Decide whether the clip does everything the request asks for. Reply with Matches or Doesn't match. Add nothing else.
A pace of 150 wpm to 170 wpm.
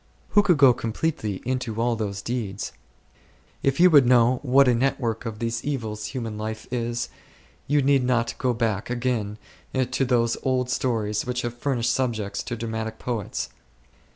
Matches